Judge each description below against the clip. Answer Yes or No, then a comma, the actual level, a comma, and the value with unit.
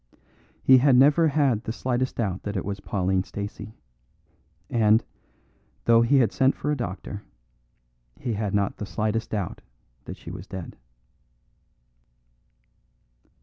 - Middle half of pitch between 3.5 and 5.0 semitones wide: Yes, average, 4.3 semitones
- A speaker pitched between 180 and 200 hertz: No, low, 110 Hz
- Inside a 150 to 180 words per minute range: No, slow, 135 wpm